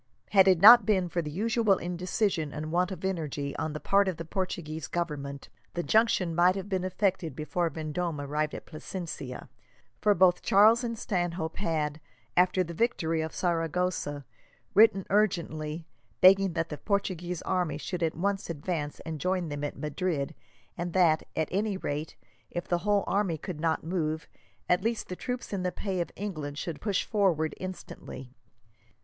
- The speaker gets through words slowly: No, average, 170 wpm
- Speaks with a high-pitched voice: No, medium, 175 Hz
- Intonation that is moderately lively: Yes, average, 3.4 semitones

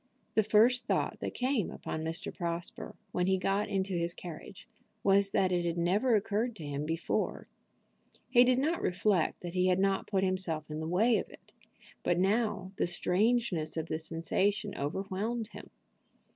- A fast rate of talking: No, average, 170 wpm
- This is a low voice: No, high, 190 Hz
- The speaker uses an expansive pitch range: No, average, 4.0 semitones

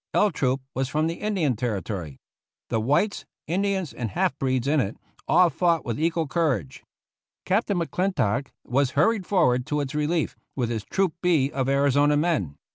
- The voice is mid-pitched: Yes, medium, 145 Hz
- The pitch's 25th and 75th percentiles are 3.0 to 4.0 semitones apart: No, wide, 5.4 semitones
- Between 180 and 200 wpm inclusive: No, average, 165 wpm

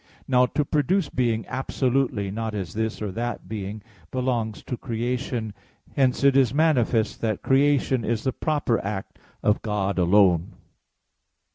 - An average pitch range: Yes, average, 3.8 semitones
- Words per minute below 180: Yes, average, 140 wpm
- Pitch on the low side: Yes, low, 115 Hz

